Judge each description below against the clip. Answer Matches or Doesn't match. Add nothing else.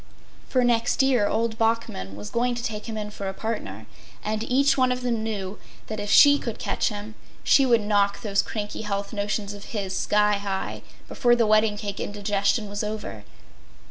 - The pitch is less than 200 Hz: Doesn't match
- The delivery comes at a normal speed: Matches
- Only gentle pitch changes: Matches